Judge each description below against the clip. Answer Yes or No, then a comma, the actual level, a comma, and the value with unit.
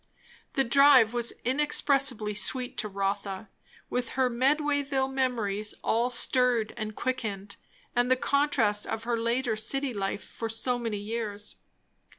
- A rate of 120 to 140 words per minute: Yes, slow, 135 wpm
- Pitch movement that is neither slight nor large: Yes, average, 3.6 semitones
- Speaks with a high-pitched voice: Yes, high, 235 Hz